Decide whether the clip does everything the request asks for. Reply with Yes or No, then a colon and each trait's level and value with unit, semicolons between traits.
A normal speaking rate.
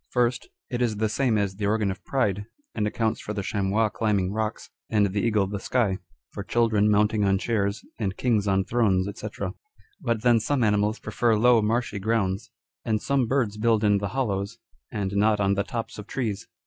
Yes: average, 195 wpm